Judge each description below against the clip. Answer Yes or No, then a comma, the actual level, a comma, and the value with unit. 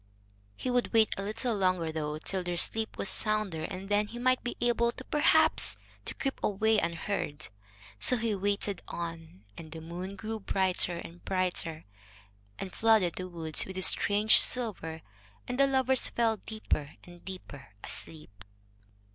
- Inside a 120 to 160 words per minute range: Yes, average, 155 wpm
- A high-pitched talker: Yes, high, 195 Hz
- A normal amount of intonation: Yes, average, 4.8 semitones